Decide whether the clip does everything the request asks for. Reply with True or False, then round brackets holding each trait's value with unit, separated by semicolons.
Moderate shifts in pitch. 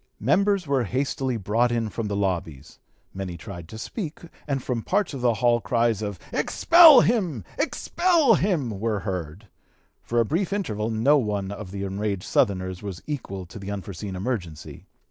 False (6.2 semitones)